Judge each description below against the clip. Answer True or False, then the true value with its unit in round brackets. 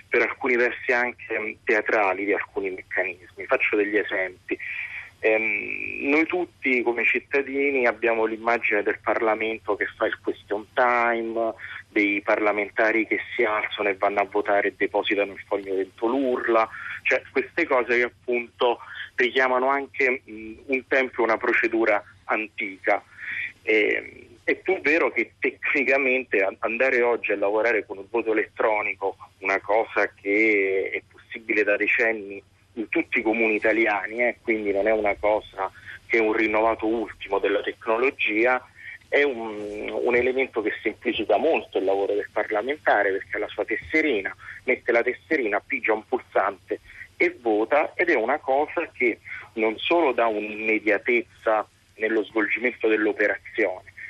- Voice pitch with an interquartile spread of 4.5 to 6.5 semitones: False (4.0 semitones)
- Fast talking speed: False (140 wpm)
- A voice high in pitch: False (115 Hz)